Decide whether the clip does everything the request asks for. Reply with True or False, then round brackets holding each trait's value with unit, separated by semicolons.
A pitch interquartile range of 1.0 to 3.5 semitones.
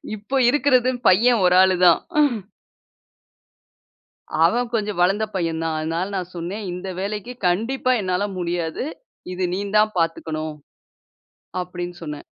False (3.9 semitones)